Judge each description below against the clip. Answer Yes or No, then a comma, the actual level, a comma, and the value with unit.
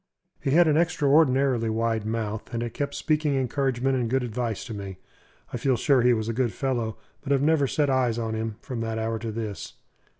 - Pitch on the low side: Yes, low, 120 Hz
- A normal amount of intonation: Yes, average, 3.4 semitones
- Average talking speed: No, fast, 210 wpm